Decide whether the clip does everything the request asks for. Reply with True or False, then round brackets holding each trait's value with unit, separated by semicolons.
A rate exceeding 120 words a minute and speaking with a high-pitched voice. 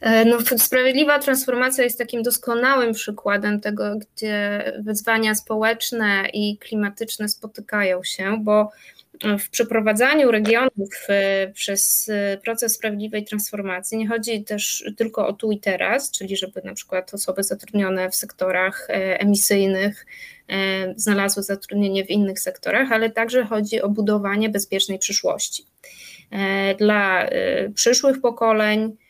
False (115 wpm; 210 Hz)